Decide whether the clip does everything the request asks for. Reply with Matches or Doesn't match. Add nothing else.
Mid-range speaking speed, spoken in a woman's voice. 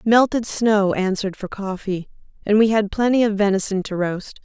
Matches